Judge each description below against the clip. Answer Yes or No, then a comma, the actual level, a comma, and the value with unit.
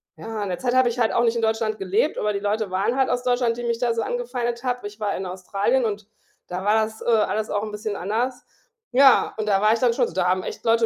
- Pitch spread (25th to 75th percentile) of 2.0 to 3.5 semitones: Yes, average, 2.8 semitones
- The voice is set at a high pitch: Yes, high, 220 Hz